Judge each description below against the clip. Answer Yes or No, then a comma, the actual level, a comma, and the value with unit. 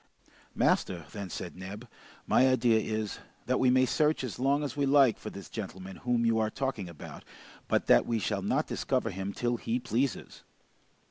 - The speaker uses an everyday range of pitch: Yes, average, 4.4 semitones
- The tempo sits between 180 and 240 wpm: Yes, average, 185 wpm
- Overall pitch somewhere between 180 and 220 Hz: No, low, 115 Hz